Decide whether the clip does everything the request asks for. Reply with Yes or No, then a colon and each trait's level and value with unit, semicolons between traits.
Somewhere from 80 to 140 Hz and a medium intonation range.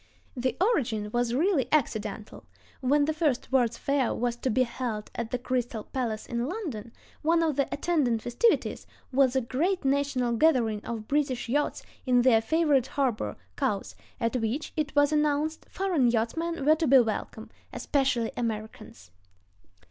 No: very high, 255 Hz; average, 4.3 semitones